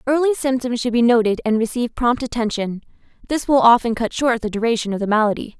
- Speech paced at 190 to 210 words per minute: Yes, fast, 205 wpm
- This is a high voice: Yes, high, 235 Hz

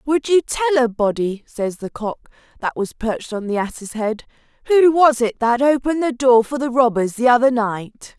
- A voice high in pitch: Yes, high, 245 Hz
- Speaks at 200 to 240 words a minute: Yes, fast, 205 wpm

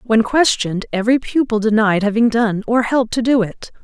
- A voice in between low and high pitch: No, high, 225 Hz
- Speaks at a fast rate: No, average, 190 wpm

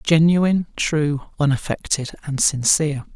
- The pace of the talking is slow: Yes, slow, 95 wpm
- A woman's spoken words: No, male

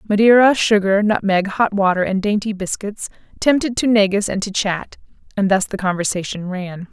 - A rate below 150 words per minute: No, average, 165 wpm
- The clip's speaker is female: Yes, female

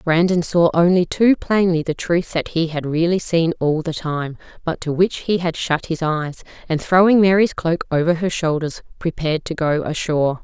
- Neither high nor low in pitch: Yes, medium, 165 Hz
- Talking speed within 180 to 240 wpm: Yes, average, 195 wpm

